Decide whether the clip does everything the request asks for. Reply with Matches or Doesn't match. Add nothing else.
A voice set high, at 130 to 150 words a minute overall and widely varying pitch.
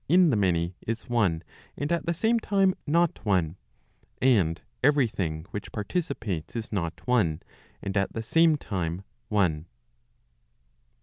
Doesn't match